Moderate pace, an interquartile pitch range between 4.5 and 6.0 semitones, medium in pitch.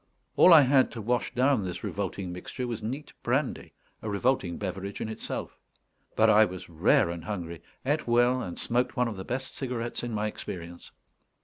No: average, 185 wpm; average, 5.2 semitones; low, 110 Hz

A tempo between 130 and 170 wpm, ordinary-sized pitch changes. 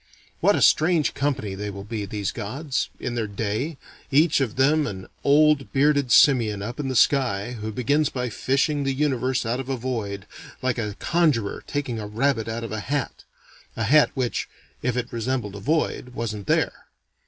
No: average, 185 wpm; average, 4.5 semitones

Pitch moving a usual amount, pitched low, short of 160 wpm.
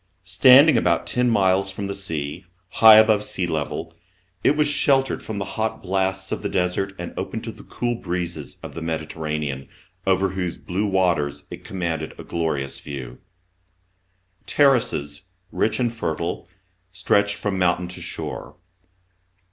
Yes: average, 4.5 semitones; very low, 95 Hz; average, 150 wpm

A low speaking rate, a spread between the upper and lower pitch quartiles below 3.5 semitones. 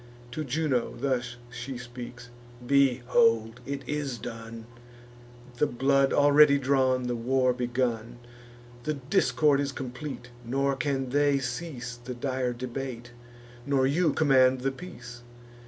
Yes: slow, 125 wpm; narrow, 2.5 semitones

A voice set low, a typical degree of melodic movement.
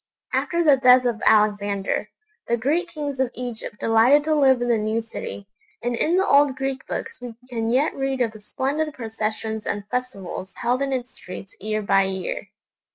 No: high, 245 Hz; average, 3.9 semitones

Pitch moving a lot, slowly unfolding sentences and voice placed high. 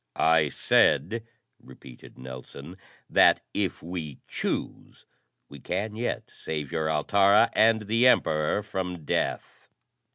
No: wide, 5.8 semitones; slow, 110 wpm; very low, 85 Hz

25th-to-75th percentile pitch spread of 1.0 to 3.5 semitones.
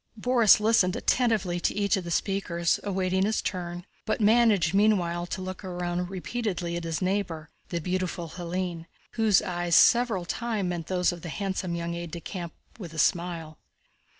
Yes: average, 2.8 semitones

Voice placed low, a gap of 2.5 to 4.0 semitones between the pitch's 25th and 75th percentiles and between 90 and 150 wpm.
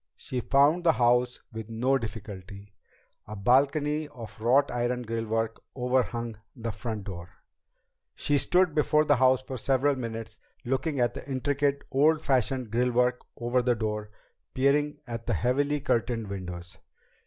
Yes: low, 125 Hz; average, 3.5 semitones; average, 145 wpm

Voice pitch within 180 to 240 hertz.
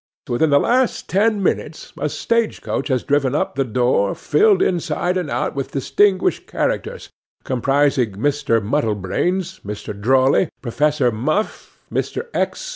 No: medium, 145 Hz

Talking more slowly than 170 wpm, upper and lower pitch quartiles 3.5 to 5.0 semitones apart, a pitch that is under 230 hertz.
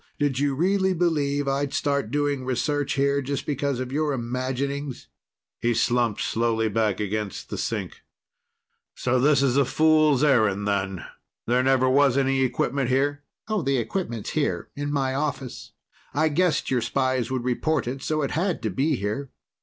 No: average, 160 wpm; average, 2.8 semitones; low, 135 Hz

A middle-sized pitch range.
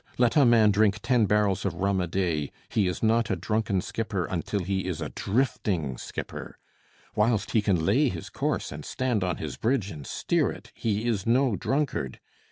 Yes: average, 4.0 semitones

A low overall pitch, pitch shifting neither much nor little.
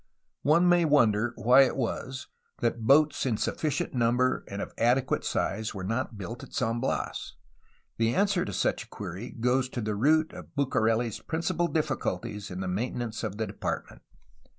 Yes: low, 120 Hz; average, 4.1 semitones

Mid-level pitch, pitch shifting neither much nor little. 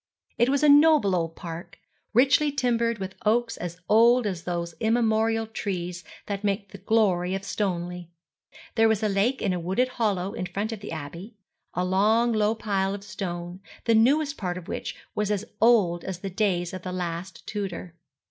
No: high, 200 Hz; average, 3.9 semitones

